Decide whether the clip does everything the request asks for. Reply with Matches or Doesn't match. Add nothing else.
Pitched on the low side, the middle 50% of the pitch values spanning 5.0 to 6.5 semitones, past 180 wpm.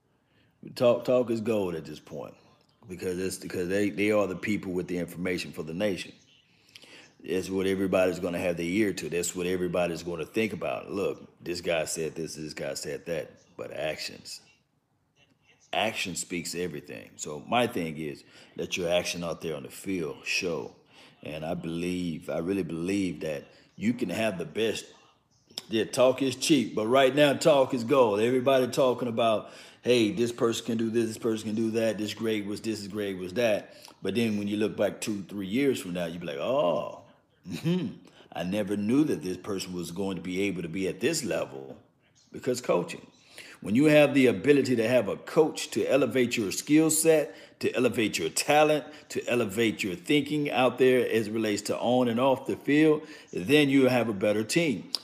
Matches